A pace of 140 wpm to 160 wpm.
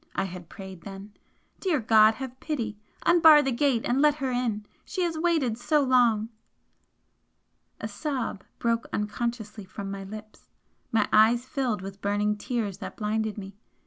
Yes: average, 155 wpm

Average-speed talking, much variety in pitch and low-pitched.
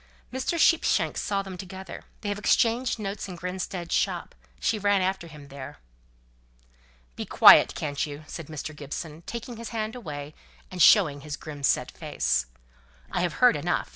No: average, 160 wpm; wide, 5.7 semitones; medium, 185 Hz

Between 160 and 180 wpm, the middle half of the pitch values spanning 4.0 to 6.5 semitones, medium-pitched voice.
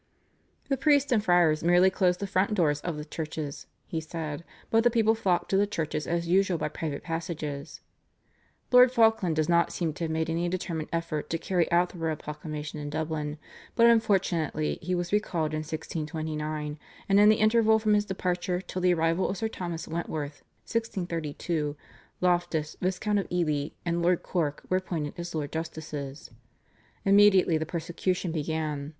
No: average, 170 wpm; average, 3.3 semitones; medium, 170 Hz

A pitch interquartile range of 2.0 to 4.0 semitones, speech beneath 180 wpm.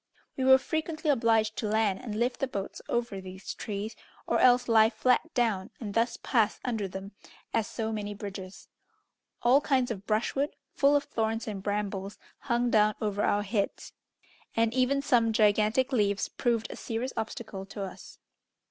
Yes: average, 3.1 semitones; average, 165 wpm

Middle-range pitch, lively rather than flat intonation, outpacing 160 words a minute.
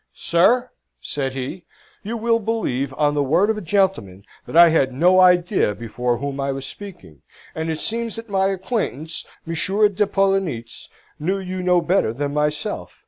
Yes: medium, 170 Hz; wide, 5.9 semitones; average, 170 wpm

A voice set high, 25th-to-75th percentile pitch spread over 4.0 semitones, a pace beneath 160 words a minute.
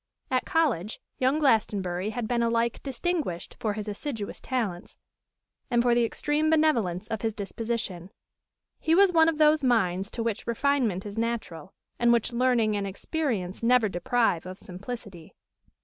Yes: high, 230 Hz; average, 4.4 semitones; average, 150 wpm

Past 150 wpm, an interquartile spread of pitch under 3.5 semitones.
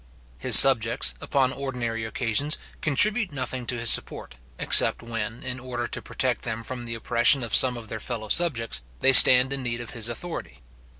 Yes: average, 180 wpm; narrow, 2.4 semitones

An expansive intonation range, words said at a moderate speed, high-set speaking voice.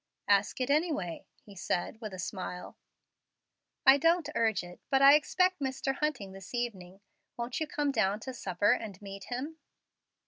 Yes: wide, 6.3 semitones; average, 165 wpm; high, 235 Hz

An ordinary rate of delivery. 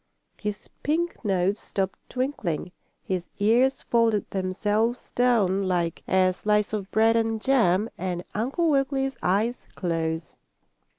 No: slow, 120 wpm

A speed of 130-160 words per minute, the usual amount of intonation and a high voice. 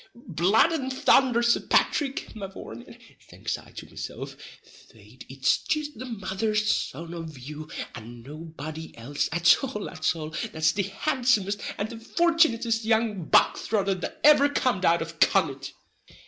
No: average, 145 wpm; wide, 7.2 semitones; high, 195 Hz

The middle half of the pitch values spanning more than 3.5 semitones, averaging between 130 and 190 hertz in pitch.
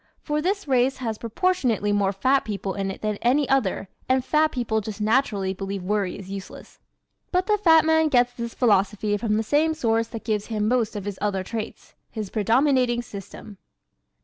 No: average, 4.5 semitones; high, 225 Hz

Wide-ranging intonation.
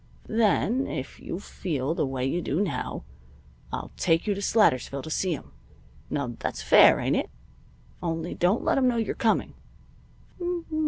Yes: wide, 7.1 semitones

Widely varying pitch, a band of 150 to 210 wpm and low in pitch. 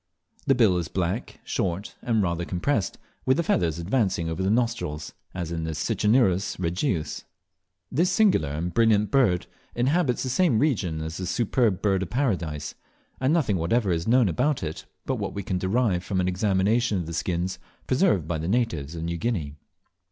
Yes: wide, 6.0 semitones; average, 175 wpm; very low, 95 Hz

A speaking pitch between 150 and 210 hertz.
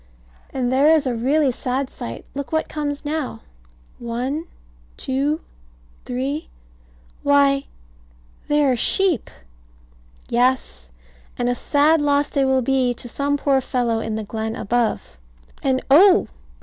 No: very high, 270 Hz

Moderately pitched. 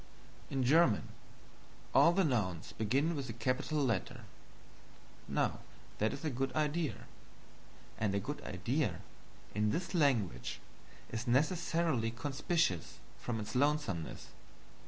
No: low, 130 Hz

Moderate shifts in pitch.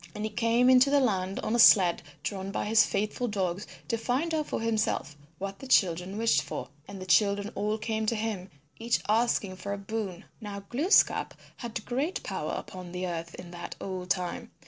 Yes: average, 3.6 semitones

